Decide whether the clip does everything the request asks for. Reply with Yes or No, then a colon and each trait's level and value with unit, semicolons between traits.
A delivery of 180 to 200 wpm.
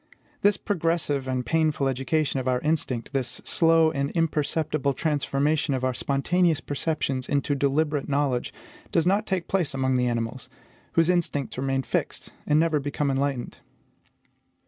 No: average, 145 wpm